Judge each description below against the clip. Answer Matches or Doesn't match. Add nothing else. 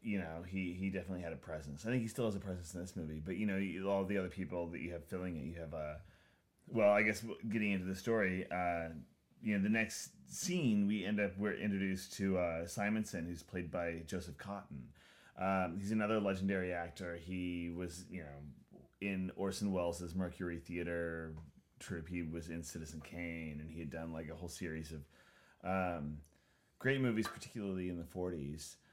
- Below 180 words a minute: Doesn't match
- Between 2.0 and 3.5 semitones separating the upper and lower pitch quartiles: Matches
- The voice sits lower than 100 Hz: Matches